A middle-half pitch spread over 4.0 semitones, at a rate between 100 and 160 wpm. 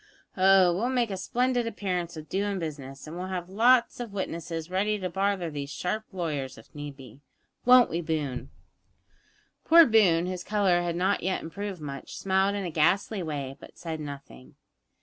No: average, 4.6 semitones; average, 175 wpm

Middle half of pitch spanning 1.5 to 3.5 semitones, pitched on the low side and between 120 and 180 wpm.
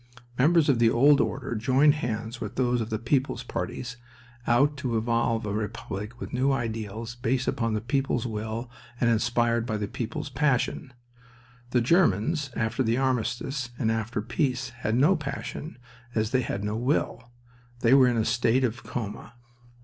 Yes: average, 2.8 semitones; low, 120 Hz; average, 170 wpm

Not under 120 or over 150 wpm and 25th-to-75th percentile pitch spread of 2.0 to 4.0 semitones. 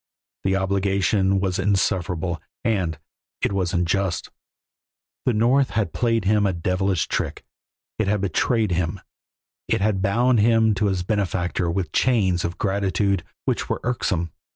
Yes: average, 140 wpm; average, 2.8 semitones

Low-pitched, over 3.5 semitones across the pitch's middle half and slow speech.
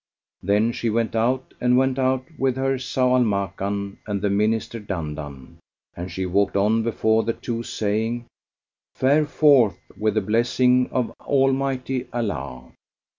No: low, 115 Hz; average, 4.0 semitones; average, 145 wpm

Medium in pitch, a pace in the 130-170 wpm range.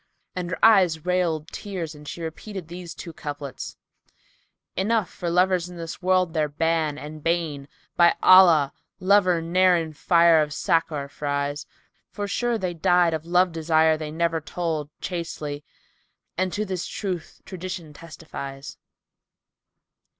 Yes: medium, 170 Hz; average, 145 wpm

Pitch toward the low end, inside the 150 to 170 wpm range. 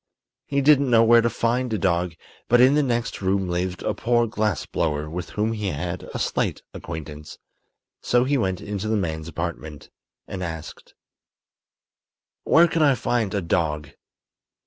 Yes: low, 100 Hz; average, 165 wpm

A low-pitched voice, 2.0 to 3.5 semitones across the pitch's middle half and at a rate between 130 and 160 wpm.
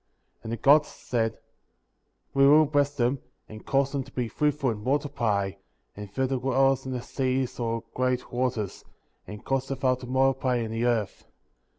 No: low, 130 Hz; average, 2.7 semitones; average, 185 wpm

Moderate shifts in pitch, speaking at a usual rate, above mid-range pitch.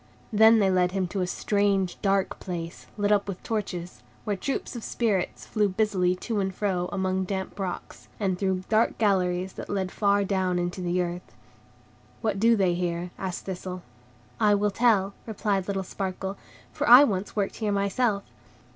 No: narrow, 2.1 semitones; average, 175 wpm; high, 195 Hz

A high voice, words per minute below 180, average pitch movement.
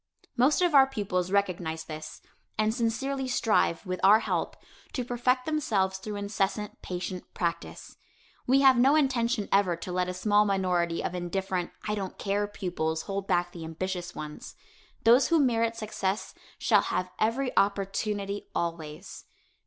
Yes: high, 200 Hz; average, 150 wpm; average, 4.4 semitones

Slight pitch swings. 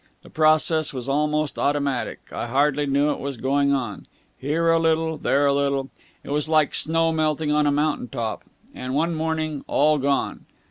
Yes: narrow, 2.1 semitones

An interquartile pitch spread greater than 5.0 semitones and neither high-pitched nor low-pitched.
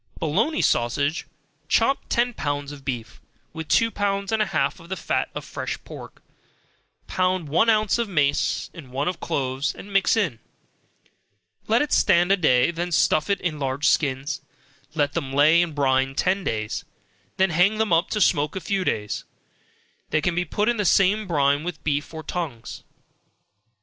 Yes: wide, 5.5 semitones; medium, 165 Hz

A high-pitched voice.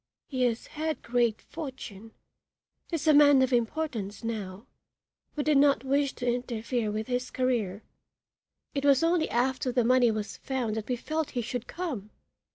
Yes: very high, 250 Hz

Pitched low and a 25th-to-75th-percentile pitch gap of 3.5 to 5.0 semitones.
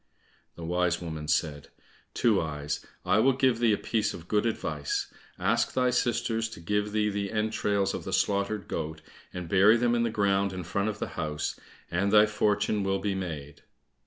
Yes: low, 100 Hz; average, 4.1 semitones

